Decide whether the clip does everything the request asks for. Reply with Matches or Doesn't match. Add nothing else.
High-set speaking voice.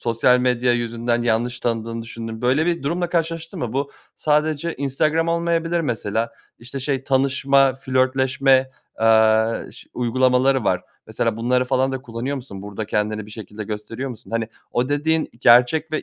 Doesn't match